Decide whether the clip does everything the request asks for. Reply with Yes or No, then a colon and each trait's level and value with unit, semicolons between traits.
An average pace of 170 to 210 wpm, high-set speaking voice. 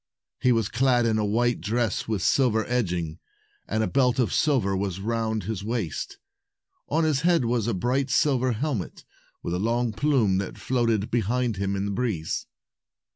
No: average, 175 wpm; low, 115 Hz